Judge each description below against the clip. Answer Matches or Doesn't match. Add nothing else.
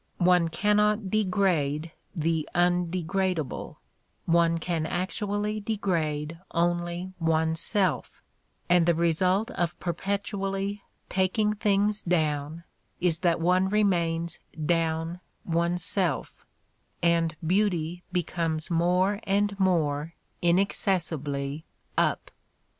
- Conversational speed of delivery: Doesn't match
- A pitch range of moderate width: Matches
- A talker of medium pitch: Matches